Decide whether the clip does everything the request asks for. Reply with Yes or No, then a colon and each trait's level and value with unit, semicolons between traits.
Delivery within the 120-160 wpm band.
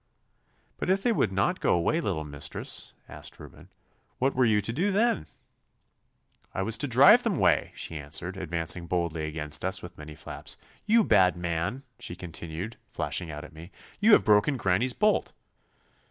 No: average, 170 wpm